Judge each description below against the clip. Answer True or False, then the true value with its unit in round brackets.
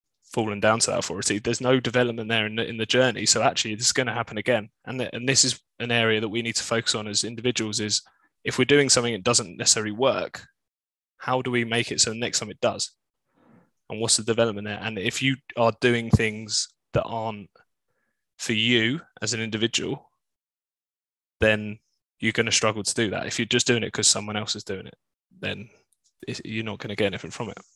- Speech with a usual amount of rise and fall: False (2.0 semitones)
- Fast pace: True (225 wpm)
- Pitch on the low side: True (115 Hz)